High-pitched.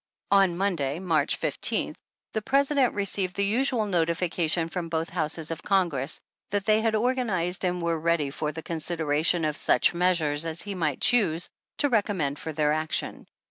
No: medium, 175 Hz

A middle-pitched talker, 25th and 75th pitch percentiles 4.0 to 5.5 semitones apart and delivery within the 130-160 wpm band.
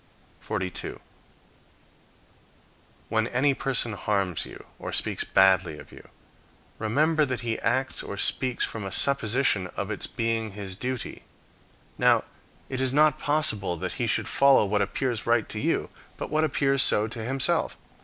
No: low, 115 Hz; average, 4.9 semitones; average, 150 wpm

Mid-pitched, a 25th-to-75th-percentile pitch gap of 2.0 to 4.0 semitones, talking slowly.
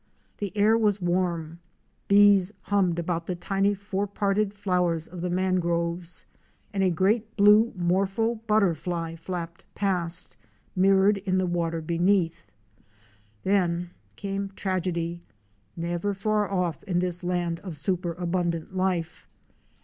Yes: medium, 180 Hz; narrow, 2.6 semitones; slow, 125 wpm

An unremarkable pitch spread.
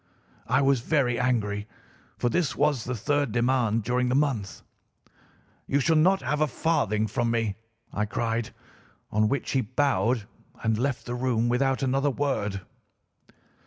Yes: average, 3.7 semitones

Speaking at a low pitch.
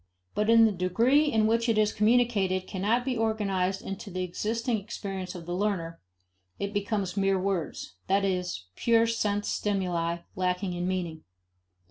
No: high, 195 Hz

